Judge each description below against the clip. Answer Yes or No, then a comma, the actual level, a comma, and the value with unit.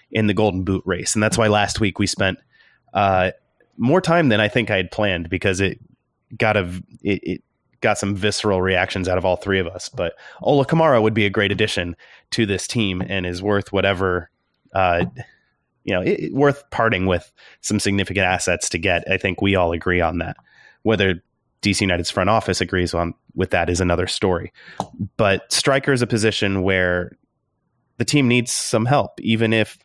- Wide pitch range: No, average, 3.4 semitones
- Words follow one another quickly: No, average, 195 wpm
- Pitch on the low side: Yes, low, 100 Hz